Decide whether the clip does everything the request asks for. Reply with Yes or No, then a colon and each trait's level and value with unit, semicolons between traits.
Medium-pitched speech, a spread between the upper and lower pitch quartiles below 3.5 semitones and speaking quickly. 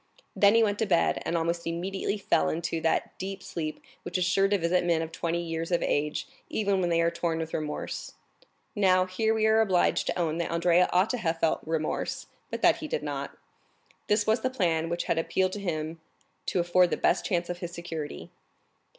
Yes: medium, 175 Hz; average, 2.9 semitones; fast, 210 wpm